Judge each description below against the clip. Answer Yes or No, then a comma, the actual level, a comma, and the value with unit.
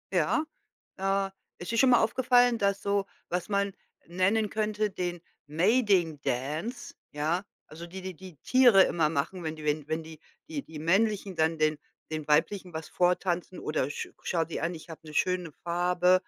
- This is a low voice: No, medium, 180 Hz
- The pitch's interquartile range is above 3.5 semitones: Yes, average, 4.0 semitones